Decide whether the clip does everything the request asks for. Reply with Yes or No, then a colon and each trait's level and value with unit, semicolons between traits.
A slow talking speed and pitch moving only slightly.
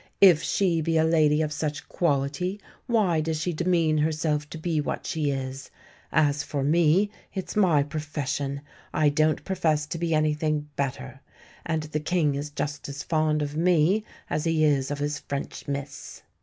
No: average, 170 wpm; narrow, 2.0 semitones